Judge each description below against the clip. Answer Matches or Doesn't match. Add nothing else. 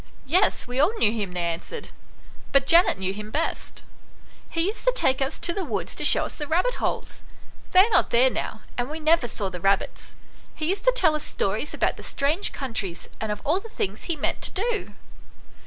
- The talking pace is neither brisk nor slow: Doesn't match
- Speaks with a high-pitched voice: Matches